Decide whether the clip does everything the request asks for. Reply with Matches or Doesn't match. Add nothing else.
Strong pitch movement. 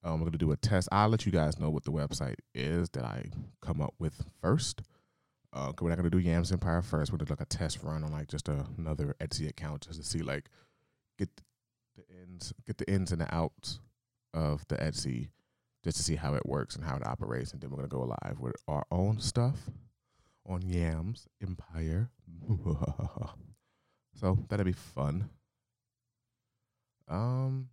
Matches